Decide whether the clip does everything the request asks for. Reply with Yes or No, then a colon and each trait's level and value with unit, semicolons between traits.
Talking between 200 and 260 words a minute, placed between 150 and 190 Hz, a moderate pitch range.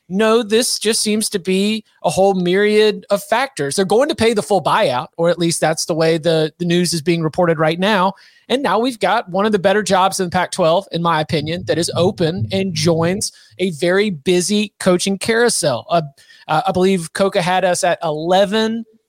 Yes: fast, 205 wpm; medium, 185 Hz; average, 3.5 semitones